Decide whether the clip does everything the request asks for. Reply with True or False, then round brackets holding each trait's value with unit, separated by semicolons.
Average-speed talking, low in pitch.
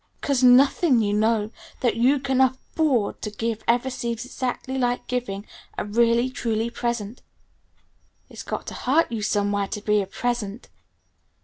False (150 wpm; 235 Hz)